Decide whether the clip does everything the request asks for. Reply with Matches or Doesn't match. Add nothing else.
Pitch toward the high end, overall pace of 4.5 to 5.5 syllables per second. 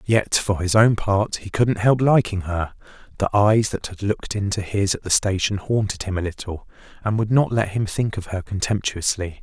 Doesn't match